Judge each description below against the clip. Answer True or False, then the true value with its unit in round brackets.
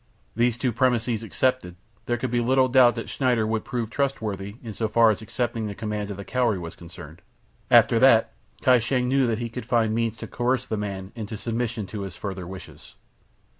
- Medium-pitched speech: False (115 Hz)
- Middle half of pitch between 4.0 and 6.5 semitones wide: False (2.9 semitones)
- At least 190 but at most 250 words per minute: True (205 wpm)